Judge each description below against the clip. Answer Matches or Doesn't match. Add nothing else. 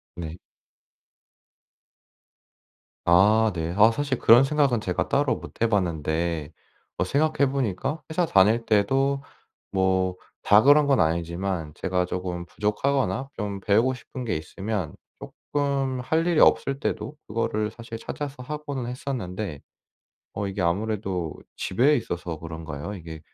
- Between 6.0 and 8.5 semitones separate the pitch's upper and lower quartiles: Matches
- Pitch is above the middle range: Doesn't match